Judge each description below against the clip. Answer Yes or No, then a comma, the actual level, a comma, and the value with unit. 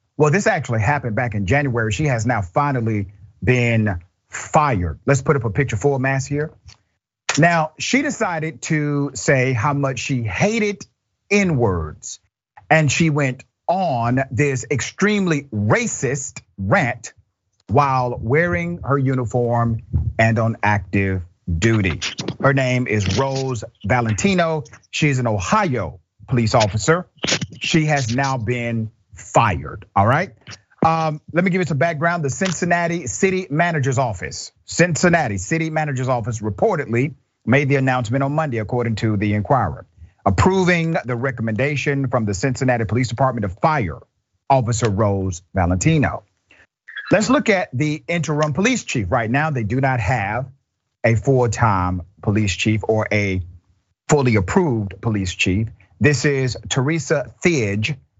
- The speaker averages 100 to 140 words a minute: Yes, slow, 135 wpm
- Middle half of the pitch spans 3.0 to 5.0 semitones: No, wide, 5.5 semitones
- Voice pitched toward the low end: Yes, low, 125 Hz